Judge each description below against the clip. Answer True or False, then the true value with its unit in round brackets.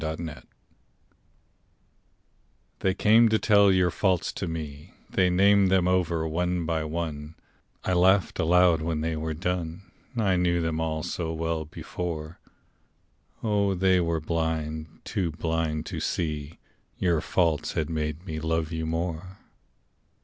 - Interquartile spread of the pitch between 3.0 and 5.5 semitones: False (2.5 semitones)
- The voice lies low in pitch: True (85 Hz)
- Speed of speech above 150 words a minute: False (135 wpm)